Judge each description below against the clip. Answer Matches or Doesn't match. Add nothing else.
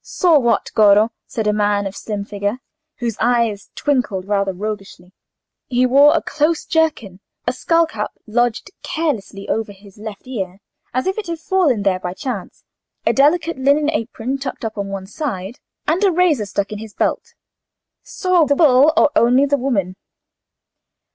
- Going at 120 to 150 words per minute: Doesn't match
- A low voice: Doesn't match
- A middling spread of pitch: Doesn't match